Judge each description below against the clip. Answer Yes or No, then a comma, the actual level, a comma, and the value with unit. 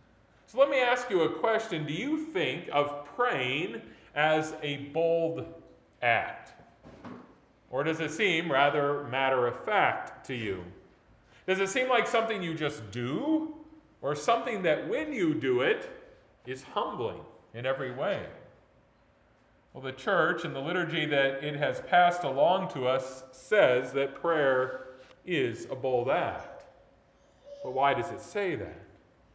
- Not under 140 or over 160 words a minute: Yes, average, 145 wpm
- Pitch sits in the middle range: Yes, medium, 165 Hz